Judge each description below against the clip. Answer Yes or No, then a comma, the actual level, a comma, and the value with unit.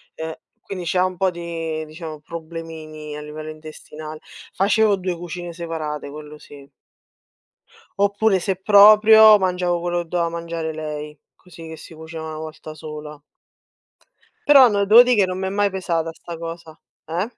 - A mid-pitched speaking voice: Yes, medium, 165 Hz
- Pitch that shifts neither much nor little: Yes, average, 3.2 semitones